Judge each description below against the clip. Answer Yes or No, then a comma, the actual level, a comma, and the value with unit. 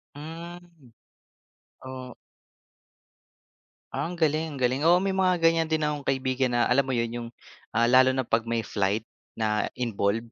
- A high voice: No, low, 130 Hz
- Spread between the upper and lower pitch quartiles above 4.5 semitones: Yes, average, 5.3 semitones